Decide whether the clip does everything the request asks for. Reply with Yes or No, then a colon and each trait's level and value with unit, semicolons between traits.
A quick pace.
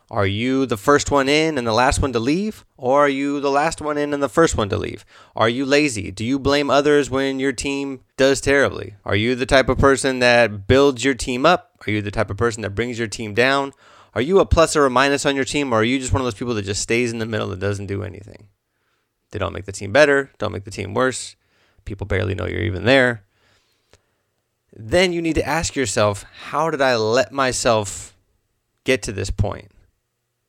Yes: fast, 235 wpm